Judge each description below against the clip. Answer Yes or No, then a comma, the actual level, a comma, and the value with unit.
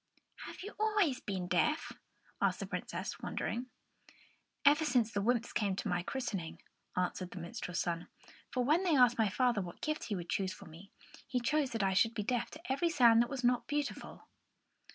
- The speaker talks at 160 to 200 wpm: Yes, average, 195 wpm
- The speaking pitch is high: Yes, high, 235 Hz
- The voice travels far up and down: Yes, wide, 6.5 semitones